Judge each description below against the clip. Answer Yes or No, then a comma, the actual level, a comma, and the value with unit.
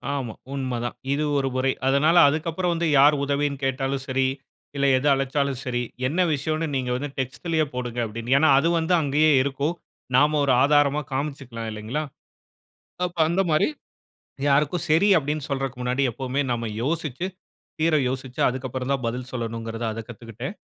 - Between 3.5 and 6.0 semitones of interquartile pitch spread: No, average, 3.0 semitones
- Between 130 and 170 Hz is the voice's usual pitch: Yes, low, 135 Hz